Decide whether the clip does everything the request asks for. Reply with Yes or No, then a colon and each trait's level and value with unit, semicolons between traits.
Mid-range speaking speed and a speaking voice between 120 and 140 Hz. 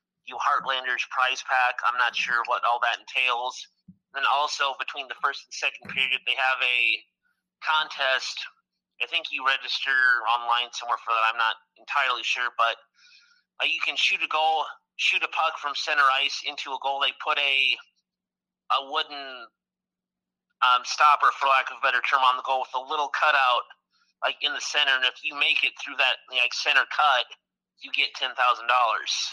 Yes: average, 180 wpm; low, 135 Hz